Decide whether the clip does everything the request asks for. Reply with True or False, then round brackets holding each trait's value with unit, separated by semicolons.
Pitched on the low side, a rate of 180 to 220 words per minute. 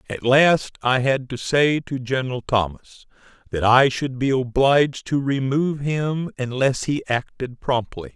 False (130 Hz; 155 wpm)